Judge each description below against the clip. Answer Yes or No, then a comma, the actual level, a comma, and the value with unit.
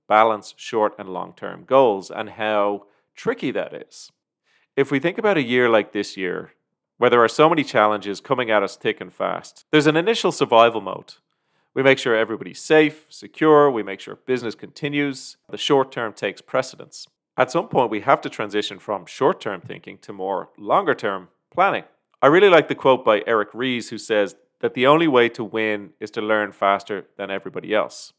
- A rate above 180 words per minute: Yes, average, 195 wpm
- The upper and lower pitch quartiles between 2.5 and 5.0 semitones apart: No, wide, 5.4 semitones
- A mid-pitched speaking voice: No, low, 115 Hz